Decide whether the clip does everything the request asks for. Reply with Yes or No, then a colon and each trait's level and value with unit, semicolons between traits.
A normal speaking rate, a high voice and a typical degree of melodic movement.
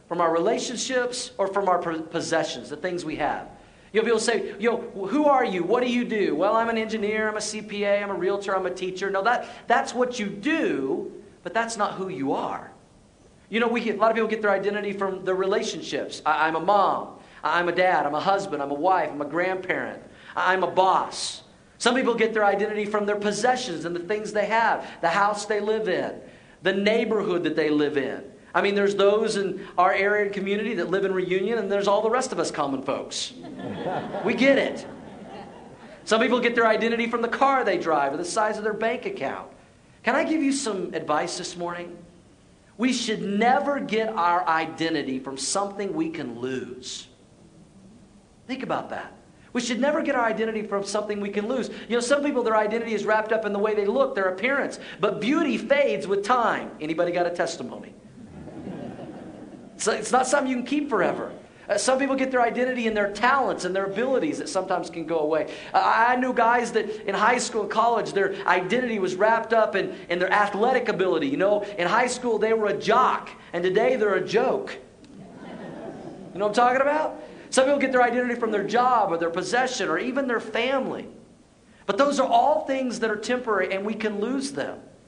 No: fast, 210 wpm; high, 210 Hz; average, 4.2 semitones